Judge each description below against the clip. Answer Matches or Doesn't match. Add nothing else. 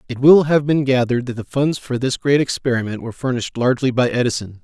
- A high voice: Doesn't match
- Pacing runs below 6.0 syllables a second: Doesn't match